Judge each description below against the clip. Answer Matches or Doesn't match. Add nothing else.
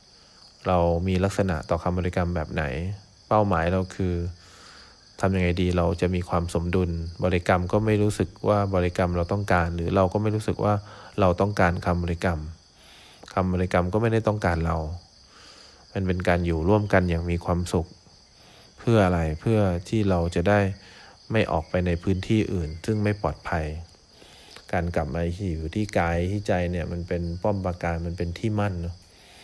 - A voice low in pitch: Matches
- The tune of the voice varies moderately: Doesn't match